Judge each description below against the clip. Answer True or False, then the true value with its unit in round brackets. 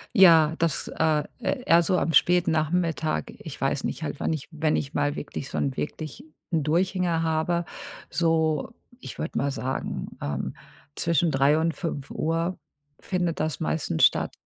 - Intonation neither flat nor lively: False (2.1 semitones)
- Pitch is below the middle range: False (160 Hz)